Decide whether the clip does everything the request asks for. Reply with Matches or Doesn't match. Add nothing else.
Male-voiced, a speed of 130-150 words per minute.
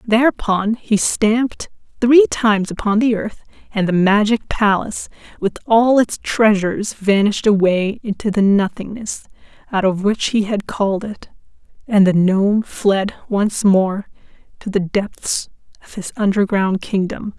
Doesn't match